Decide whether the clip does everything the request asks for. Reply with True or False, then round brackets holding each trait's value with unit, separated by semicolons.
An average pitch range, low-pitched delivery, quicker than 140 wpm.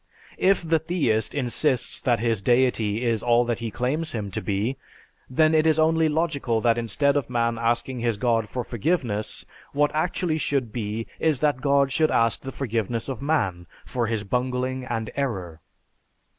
True (4.2 semitones; 125 Hz; 170 wpm)